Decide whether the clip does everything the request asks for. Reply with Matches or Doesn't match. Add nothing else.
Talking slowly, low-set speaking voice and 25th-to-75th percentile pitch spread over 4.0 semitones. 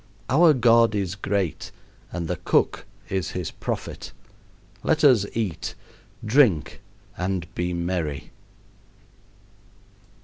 Matches